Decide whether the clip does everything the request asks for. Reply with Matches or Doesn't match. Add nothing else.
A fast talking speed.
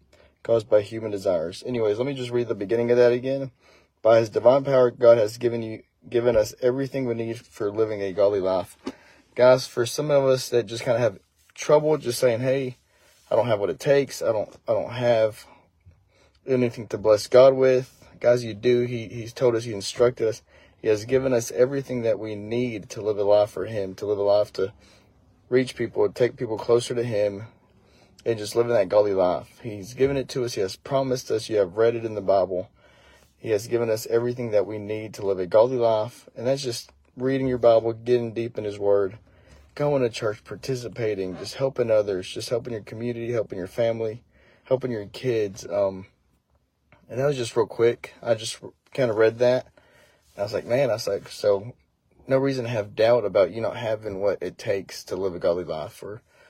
Matches